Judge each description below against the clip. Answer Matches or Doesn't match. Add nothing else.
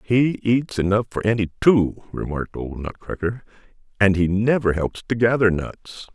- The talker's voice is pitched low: Matches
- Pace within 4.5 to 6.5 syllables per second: Matches